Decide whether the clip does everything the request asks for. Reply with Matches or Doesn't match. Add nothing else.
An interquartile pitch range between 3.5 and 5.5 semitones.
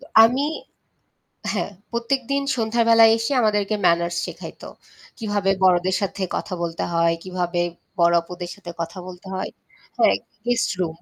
Matches